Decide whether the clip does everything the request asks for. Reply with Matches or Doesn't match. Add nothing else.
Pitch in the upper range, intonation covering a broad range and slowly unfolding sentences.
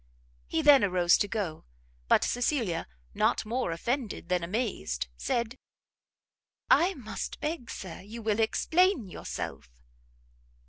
Matches